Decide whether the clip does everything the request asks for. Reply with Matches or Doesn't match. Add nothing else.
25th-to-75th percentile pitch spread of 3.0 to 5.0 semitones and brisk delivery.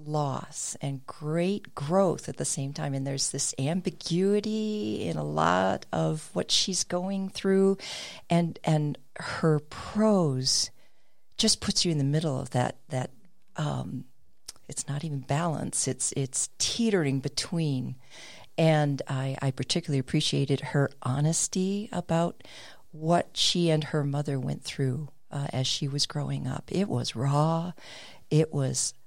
Doesn't match